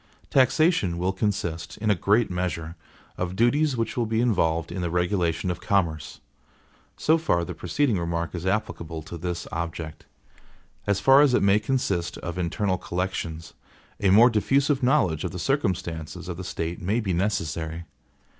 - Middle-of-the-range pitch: No, very low, 90 Hz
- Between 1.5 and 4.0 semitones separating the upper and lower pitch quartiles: No, average, 4.7 semitones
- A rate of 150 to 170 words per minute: Yes, average, 165 wpm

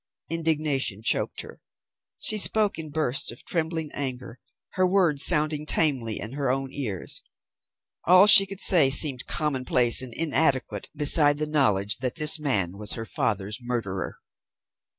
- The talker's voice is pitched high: No, medium, 140 Hz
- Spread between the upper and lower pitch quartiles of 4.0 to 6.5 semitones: Yes, average, 4.6 semitones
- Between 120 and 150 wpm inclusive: Yes, average, 145 wpm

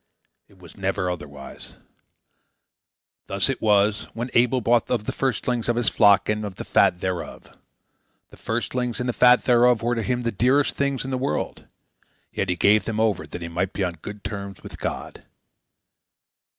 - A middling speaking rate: Yes, average, 180 wpm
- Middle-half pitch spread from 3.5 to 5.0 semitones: Yes, average, 3.9 semitones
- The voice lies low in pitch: Yes, low, 110 Hz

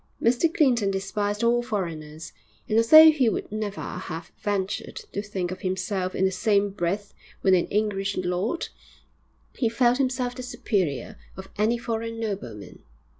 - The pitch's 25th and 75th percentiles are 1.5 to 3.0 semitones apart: No, average, 3.8 semitones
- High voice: Yes, high, 205 Hz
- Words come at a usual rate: Yes, average, 150 wpm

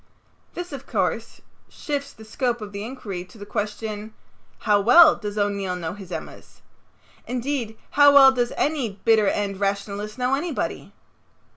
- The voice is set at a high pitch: Yes, high, 220 Hz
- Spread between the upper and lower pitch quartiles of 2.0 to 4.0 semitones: No, average, 4.6 semitones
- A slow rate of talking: No, average, 150 wpm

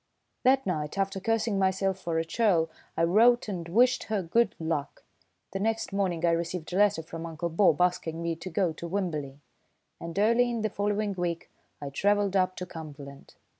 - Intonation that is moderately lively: Yes, average, 3.8 semitones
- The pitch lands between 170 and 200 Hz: Yes, medium, 185 Hz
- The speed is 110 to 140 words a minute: No, average, 185 wpm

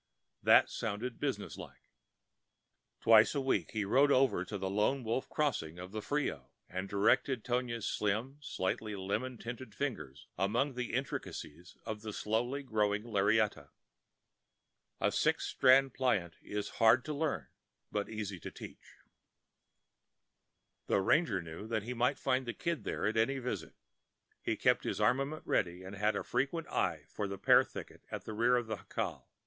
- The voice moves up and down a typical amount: Yes, average, 4.2 semitones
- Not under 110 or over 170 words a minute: Yes, average, 160 wpm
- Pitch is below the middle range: Yes, low, 110 Hz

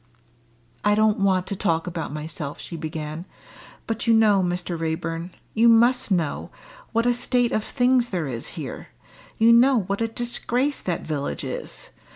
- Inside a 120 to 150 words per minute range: No, average, 165 wpm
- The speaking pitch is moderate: No, high, 200 Hz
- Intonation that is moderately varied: No, wide, 6.0 semitones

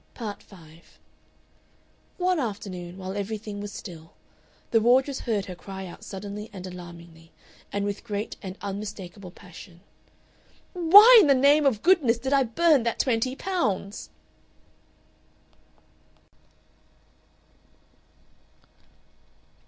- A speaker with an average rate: No, slow, 105 wpm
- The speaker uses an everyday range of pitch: No, wide, 5.7 semitones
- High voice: Yes, high, 205 Hz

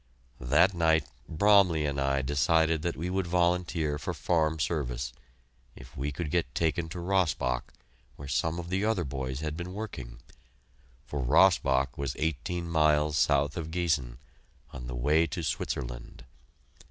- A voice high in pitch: No, very low, 80 Hz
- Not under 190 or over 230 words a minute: No, average, 150 wpm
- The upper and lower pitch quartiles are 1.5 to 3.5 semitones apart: No, average, 4.0 semitones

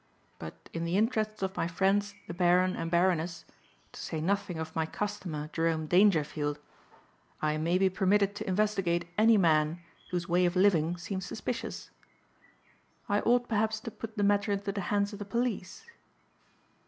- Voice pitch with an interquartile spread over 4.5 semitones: No, average, 3.5 semitones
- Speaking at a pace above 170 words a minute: No, average, 165 wpm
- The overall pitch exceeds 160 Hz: Yes, medium, 185 Hz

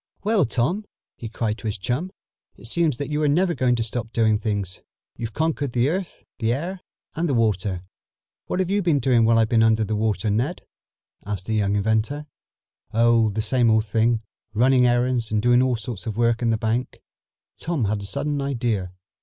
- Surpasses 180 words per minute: Yes, average, 195 wpm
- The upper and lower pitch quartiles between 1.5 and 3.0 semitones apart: No, average, 4.0 semitones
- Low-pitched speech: Yes, low, 115 Hz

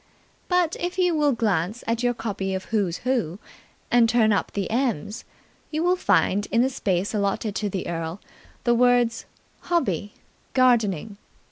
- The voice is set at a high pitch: Yes, high, 225 Hz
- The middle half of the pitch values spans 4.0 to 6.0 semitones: Yes, average, 4.3 semitones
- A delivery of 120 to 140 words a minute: No, average, 155 wpm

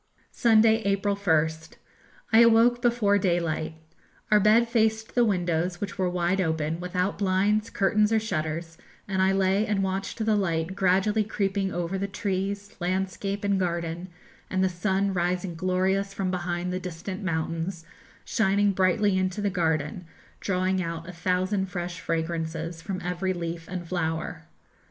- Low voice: No, medium, 185 Hz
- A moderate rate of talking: Yes, average, 150 wpm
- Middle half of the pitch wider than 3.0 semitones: No, average, 2.7 semitones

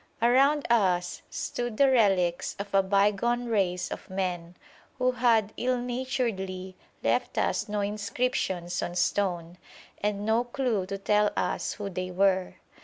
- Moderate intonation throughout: Yes, average, 4.4 semitones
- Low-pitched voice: No, high, 205 Hz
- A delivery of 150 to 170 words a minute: No, average, 140 wpm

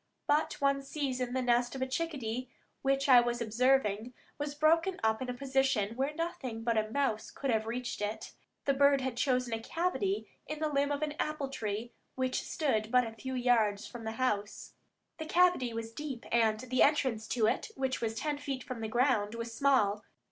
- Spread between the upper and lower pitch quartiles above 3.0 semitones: Yes, average, 3.7 semitones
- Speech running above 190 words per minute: Yes, average, 200 wpm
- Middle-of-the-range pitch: No, very high, 255 Hz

